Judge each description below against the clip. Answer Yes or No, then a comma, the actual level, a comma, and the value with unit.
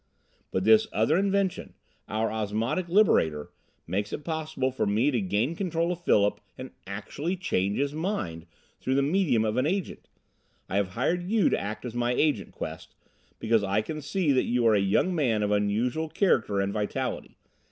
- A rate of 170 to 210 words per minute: Yes, average, 180 wpm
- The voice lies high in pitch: No, low, 120 Hz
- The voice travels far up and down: Yes, wide, 7.9 semitones